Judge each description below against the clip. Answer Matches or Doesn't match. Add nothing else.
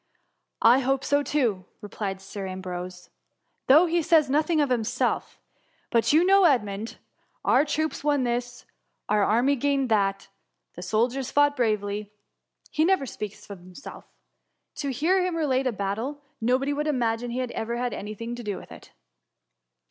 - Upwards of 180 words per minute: Matches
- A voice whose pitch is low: Doesn't match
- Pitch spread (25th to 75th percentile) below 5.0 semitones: Doesn't match